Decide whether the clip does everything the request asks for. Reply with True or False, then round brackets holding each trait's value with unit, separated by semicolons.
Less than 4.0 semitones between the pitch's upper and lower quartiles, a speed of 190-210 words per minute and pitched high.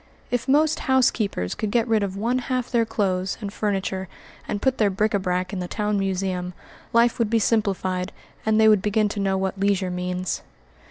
True (3.2 semitones; 200 wpm; 205 Hz)